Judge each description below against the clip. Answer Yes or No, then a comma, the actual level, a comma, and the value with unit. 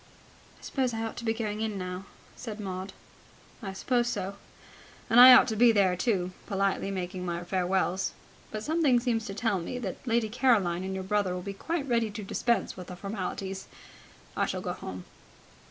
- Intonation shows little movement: No, average, 3.8 semitones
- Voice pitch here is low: No, high, 205 Hz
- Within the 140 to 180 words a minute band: No, average, 190 wpm